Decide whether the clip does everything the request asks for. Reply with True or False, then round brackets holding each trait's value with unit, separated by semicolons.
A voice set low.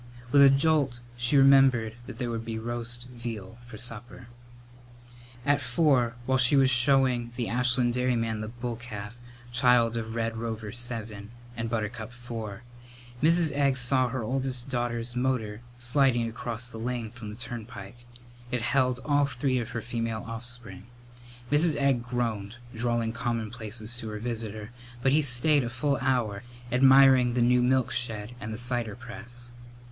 True (120 Hz)